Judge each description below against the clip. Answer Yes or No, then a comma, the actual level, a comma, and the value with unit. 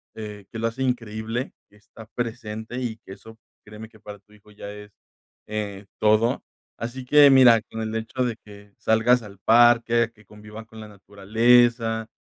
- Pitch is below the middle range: Yes, low, 110 Hz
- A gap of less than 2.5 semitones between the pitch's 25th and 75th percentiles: Yes, narrow, 2.0 semitones